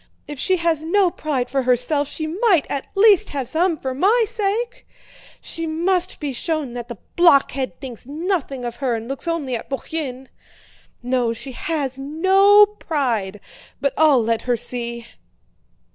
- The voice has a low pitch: No, very high, 290 Hz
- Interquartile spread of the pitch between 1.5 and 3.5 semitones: No, wide, 5.5 semitones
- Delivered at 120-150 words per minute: No, average, 160 wpm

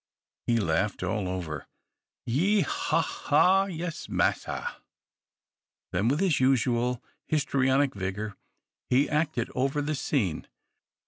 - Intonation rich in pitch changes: Yes, wide, 6.4 semitones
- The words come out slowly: Yes, slow, 110 wpm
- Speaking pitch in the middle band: No, low, 130 Hz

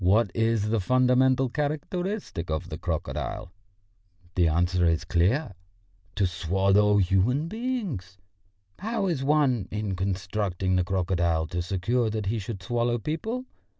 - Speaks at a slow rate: Yes, slow, 130 wpm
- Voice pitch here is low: Yes, low, 105 Hz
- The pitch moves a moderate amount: No, wide, 6.3 semitones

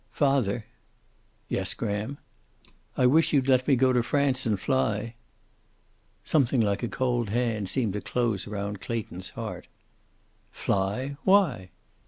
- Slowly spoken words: Yes, slow, 130 wpm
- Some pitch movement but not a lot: Yes, average, 4.3 semitones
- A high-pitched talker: No, low, 120 Hz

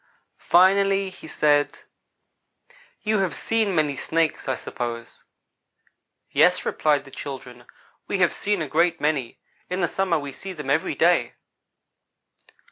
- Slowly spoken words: Yes, slow, 130 wpm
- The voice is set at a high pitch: No, medium, 160 Hz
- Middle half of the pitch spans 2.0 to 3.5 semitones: No, average, 5.3 semitones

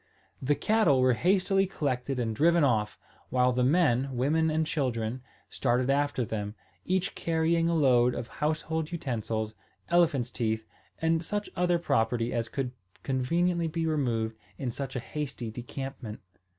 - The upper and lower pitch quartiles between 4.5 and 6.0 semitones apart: Yes, average, 5.2 semitones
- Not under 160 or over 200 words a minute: No, average, 145 wpm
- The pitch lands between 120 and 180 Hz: Yes, low, 135 Hz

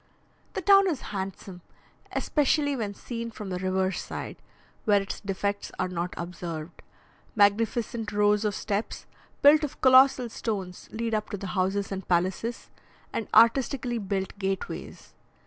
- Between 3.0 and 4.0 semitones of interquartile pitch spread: Yes, average, 3.7 semitones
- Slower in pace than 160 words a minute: Yes, average, 140 wpm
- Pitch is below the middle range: No, high, 205 Hz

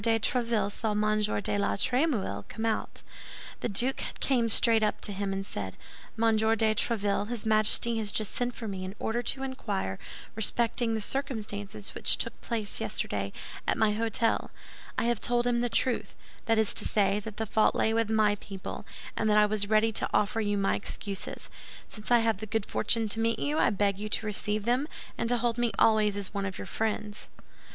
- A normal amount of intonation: No, narrow, 2.1 semitones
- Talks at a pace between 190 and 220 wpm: Yes, fast, 205 wpm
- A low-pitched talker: No, high, 220 Hz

